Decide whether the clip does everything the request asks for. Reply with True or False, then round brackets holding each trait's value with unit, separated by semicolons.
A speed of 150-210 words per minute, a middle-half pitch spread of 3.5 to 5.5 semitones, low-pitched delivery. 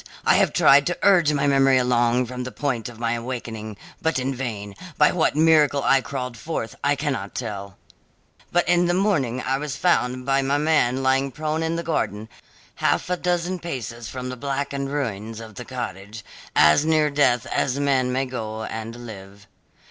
True (185 wpm; 3.9 semitones; 130 Hz)